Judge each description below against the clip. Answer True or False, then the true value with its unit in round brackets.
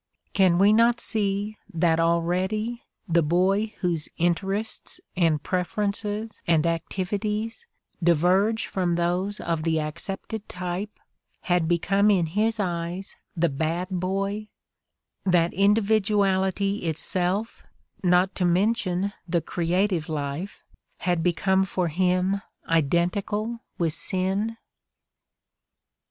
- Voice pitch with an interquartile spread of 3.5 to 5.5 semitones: False (3.1 semitones)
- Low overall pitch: False (185 Hz)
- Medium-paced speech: False (105 wpm)